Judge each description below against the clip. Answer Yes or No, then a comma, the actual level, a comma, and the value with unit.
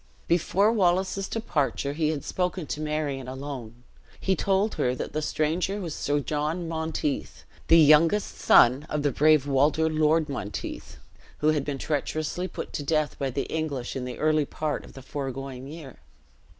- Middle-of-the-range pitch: Yes, medium, 150 Hz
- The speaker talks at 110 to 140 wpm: No, average, 165 wpm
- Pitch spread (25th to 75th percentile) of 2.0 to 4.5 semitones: Yes, average, 2.9 semitones